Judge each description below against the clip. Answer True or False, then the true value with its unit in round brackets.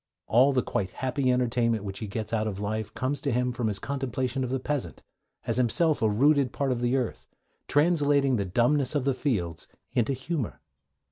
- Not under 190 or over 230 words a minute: True (195 wpm)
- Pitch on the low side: True (125 Hz)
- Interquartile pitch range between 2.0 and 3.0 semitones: False (4.0 semitones)